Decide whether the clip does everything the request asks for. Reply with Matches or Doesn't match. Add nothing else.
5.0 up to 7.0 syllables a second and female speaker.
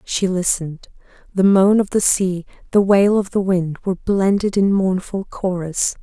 Doesn't match